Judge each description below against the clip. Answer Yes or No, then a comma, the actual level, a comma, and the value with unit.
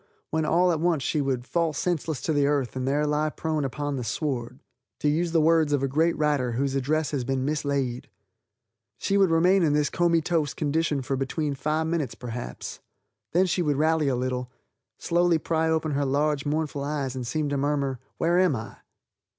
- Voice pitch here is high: No, medium, 150 Hz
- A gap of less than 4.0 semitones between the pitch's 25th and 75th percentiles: Yes, average, 3.0 semitones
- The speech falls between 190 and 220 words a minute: Yes, average, 195 wpm